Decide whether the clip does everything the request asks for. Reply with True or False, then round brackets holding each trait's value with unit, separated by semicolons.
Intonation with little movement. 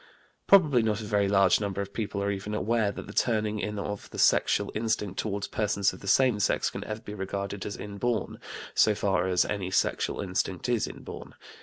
True (1.5 semitones)